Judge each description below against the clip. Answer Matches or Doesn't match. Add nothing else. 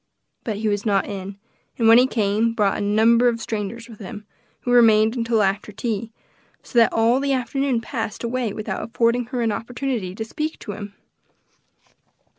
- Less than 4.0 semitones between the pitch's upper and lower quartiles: Matches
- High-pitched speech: Matches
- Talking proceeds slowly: Doesn't match